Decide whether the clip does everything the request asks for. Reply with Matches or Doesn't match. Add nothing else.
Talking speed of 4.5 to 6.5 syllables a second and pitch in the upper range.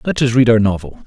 Doesn't match